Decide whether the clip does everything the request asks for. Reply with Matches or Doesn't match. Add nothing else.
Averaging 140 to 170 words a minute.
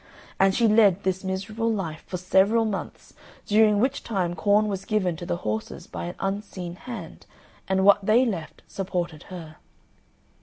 Matches